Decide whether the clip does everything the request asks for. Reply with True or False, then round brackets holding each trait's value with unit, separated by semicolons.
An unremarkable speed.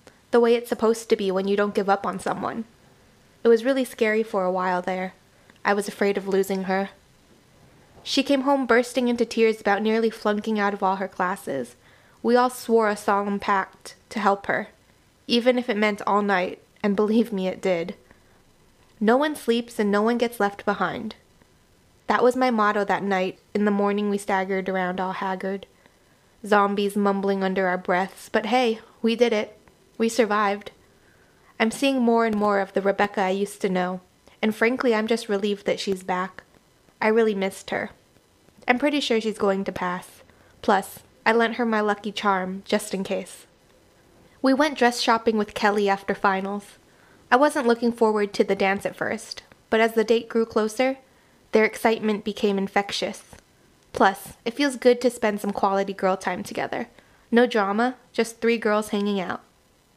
True (180 wpm)